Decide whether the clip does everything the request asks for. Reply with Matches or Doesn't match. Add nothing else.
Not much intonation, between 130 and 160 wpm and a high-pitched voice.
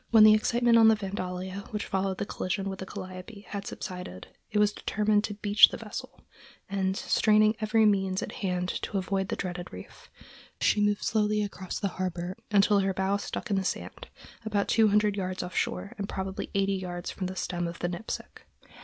Doesn't match